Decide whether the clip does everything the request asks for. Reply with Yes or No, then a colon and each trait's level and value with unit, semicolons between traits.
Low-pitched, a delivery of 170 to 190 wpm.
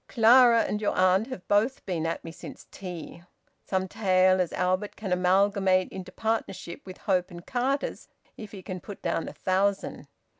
No: high, 190 Hz; average, 175 wpm